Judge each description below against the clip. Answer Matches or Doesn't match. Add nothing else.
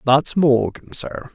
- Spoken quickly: Doesn't match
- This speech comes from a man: Matches